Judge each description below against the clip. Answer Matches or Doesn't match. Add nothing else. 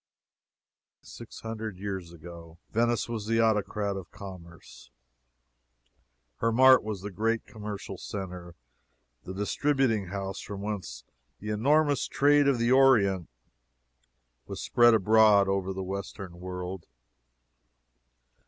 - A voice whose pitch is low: Matches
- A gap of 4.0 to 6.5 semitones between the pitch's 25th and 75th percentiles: Doesn't match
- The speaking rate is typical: Doesn't match